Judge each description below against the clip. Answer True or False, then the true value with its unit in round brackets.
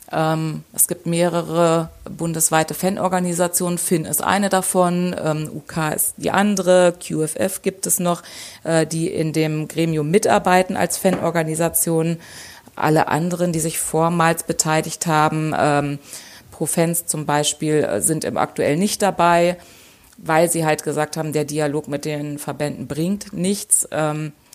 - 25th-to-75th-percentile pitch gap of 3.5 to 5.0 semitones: False (2.5 semitones)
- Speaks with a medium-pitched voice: True (165 Hz)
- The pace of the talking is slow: True (120 wpm)